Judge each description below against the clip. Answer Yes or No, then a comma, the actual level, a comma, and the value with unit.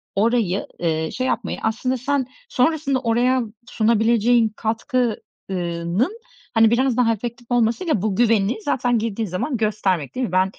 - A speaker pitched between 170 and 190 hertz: No, high, 230 Hz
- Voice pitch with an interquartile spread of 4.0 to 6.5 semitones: No, average, 3.5 semitones